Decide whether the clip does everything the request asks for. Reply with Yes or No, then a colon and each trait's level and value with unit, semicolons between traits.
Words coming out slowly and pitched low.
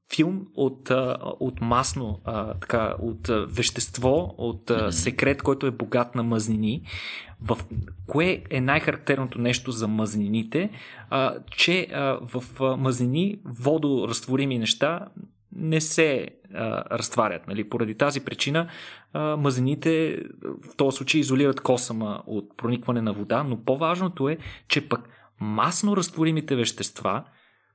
Yes: slow, 110 wpm; low, 130 Hz